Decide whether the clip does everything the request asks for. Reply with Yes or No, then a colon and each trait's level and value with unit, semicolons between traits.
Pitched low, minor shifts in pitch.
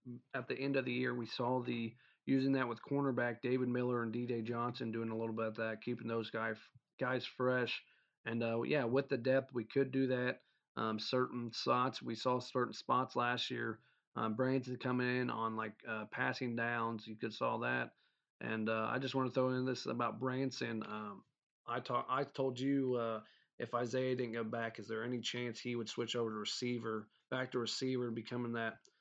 Yes: low, 120 Hz; narrow, 2.0 semitones